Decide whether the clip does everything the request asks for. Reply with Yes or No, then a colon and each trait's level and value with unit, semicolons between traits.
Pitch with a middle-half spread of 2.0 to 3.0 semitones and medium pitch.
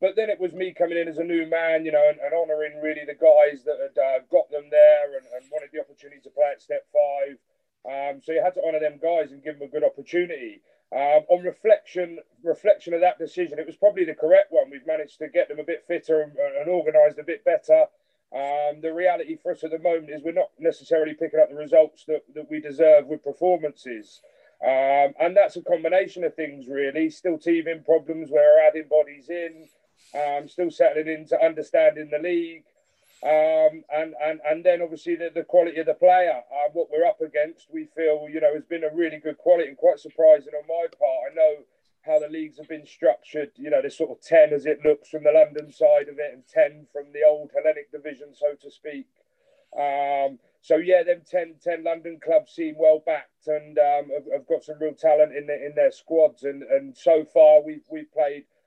No: average, 4.7 semitones; medium, 160 Hz